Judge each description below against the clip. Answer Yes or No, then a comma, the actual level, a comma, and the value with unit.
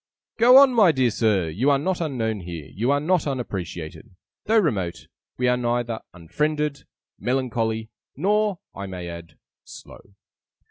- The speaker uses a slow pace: No, average, 145 wpm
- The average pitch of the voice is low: Yes, low, 120 Hz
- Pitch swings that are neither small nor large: No, wide, 7.6 semitones